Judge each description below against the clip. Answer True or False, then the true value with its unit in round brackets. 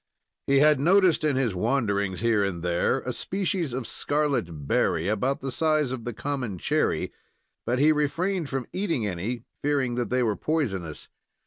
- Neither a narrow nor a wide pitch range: False (6.3 semitones)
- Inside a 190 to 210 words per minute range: False (165 wpm)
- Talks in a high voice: False (130 Hz)